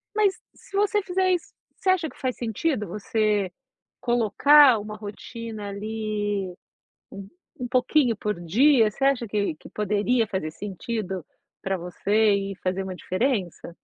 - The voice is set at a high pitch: Yes, high, 215 Hz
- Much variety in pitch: No, average, 4.3 semitones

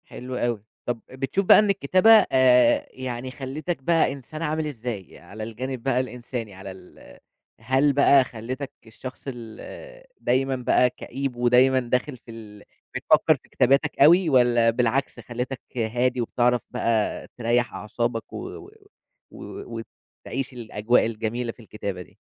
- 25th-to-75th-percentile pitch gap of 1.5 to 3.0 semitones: Yes, average, 2.7 semitones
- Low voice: Yes, low, 125 Hz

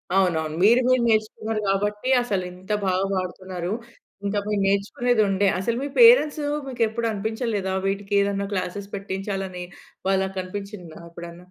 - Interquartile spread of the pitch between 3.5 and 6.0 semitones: No, narrow, 2.5 semitones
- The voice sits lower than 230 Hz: Yes, high, 200 Hz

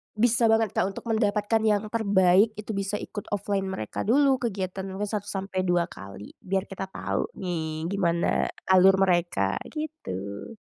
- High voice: Yes, high, 195 Hz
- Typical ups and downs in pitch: Yes, average, 3.3 semitones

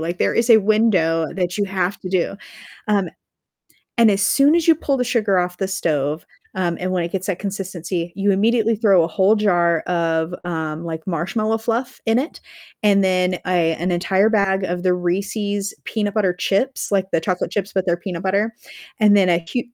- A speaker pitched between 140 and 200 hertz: Yes, high, 190 Hz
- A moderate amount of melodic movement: Yes, average, 3.1 semitones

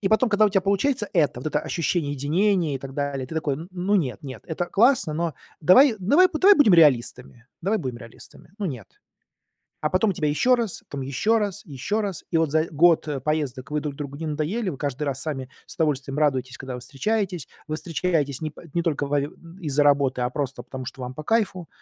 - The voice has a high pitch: No, medium, 155 Hz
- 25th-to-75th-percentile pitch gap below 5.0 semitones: No, wide, 5.4 semitones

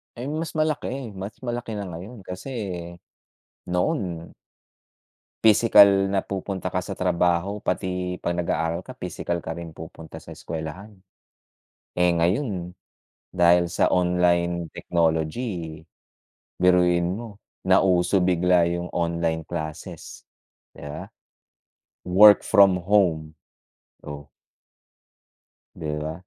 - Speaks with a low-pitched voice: Yes, very low, 90 Hz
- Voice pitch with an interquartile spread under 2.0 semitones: No, average, 2.9 semitones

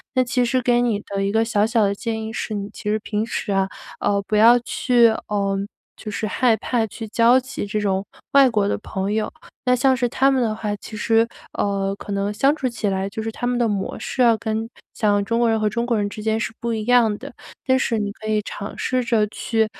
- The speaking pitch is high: Yes, high, 220 Hz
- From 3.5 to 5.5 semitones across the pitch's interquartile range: No, narrow, 2.6 semitones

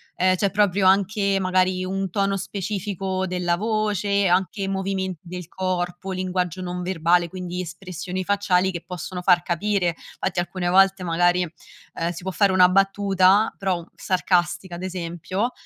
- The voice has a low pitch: No, medium, 185 Hz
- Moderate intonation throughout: No, narrow, 1.6 semitones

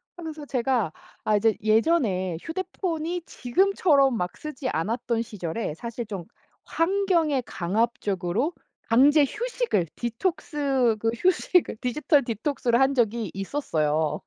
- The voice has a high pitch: Yes, high, 245 Hz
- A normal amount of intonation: No, wide, 6.4 semitones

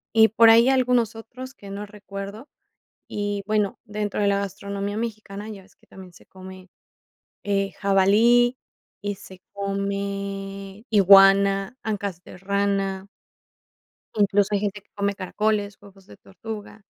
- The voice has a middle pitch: No, high, 200 Hz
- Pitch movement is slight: Yes, narrow, 1.4 semitones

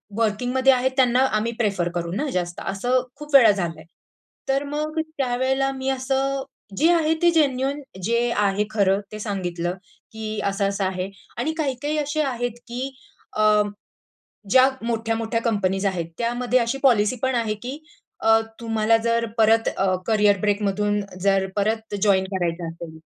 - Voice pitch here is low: No, high, 225 Hz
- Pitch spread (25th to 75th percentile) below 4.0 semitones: No, average, 4.7 semitones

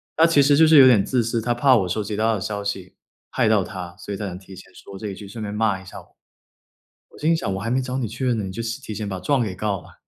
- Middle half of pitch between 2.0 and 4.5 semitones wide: Yes, average, 4.2 semitones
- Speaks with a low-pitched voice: Yes, low, 110 Hz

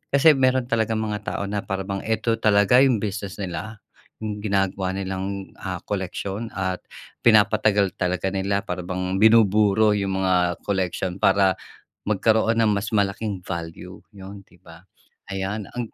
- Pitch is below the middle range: Yes, low, 100 Hz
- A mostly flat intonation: Yes, narrow, 2.3 semitones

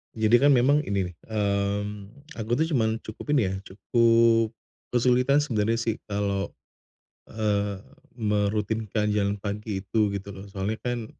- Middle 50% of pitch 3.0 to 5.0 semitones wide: No, narrow, 2.5 semitones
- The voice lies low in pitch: Yes, low, 110 Hz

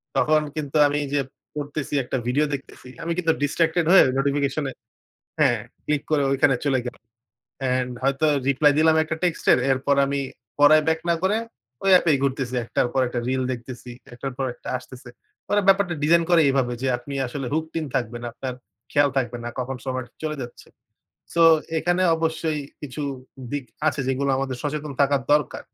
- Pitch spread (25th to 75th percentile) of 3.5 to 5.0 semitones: No, average, 3.0 semitones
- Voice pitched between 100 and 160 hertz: Yes, medium, 140 Hz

